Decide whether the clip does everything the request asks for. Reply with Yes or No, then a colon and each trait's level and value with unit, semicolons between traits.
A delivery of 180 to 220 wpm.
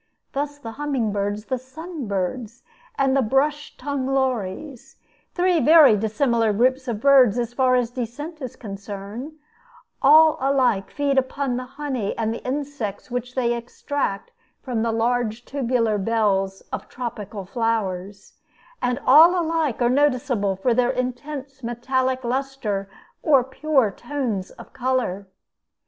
No: slow, 135 wpm